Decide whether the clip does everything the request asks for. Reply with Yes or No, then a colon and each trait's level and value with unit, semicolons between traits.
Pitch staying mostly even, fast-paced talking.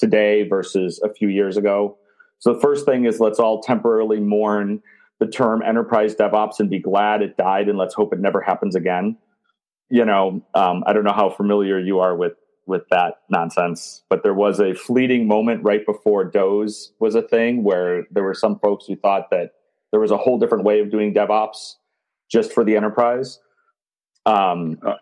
No: narrow, 2.3 semitones; average, 190 wpm